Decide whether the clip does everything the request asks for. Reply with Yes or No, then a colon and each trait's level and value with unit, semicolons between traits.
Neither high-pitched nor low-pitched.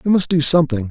Yes: medium, 155 Hz